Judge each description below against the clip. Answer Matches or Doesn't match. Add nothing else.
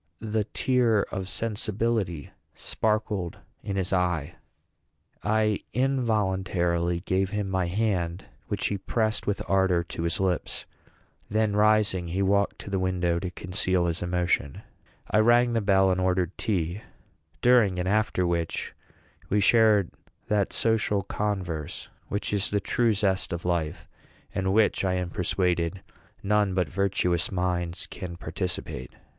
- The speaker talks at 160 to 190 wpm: Doesn't match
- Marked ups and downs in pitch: Doesn't match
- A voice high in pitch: Doesn't match